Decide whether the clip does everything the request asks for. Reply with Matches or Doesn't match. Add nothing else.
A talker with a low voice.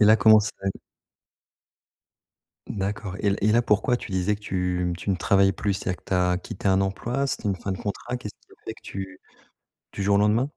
Matches